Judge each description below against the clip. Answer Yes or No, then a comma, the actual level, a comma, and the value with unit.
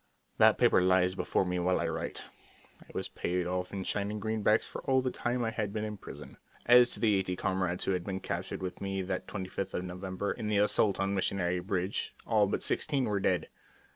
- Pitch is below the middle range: Yes, very low, 95 Hz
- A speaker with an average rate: No, fast, 220 wpm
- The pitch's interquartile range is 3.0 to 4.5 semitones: No, narrow, 2.6 semitones